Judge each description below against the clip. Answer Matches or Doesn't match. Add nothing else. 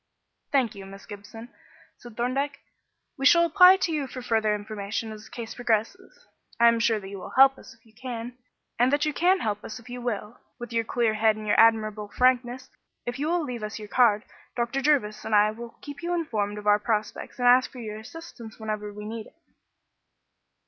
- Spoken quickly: Matches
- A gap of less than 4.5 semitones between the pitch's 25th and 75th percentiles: Matches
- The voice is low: Doesn't match